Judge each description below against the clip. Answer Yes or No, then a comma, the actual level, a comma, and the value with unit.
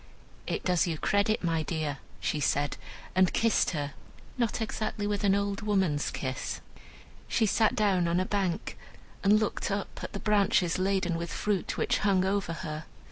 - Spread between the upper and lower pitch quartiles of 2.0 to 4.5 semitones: Yes, average, 3.6 semitones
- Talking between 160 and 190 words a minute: Yes, average, 170 wpm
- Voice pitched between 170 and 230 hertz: Yes, high, 190 Hz